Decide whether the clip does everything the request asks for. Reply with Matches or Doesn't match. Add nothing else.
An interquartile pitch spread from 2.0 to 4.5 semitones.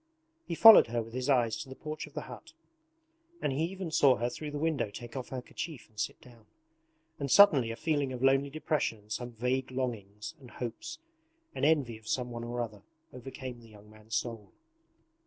Matches